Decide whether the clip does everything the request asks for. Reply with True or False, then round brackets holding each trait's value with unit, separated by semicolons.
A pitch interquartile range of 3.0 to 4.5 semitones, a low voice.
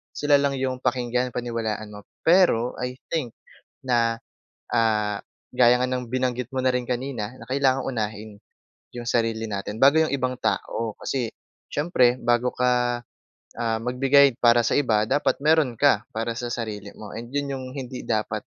False (2.4 semitones; 125 Hz)